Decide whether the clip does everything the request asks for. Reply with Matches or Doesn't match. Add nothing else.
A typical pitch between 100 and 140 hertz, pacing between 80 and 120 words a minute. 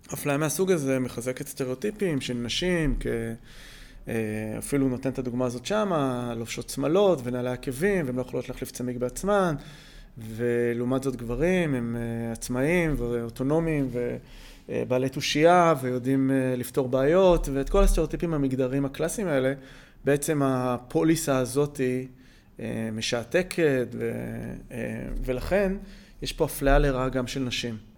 Matches